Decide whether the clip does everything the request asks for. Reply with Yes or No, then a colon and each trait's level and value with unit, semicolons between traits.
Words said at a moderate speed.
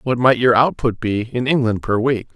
No: fast, 230 wpm